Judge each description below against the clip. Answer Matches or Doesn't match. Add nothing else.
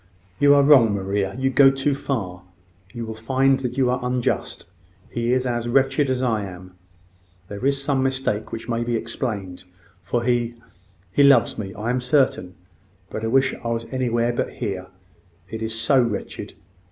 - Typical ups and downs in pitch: Matches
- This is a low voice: Matches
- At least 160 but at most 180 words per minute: Matches